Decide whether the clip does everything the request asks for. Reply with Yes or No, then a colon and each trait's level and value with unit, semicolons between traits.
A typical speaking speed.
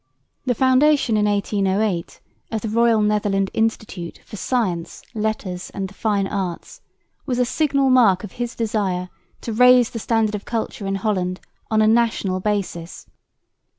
Yes: average, 150 wpm